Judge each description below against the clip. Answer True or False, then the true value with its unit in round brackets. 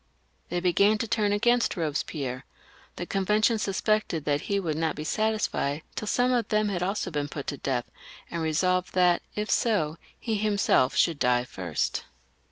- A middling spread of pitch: False (5.9 semitones)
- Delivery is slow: False (175 wpm)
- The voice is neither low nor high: True (180 Hz)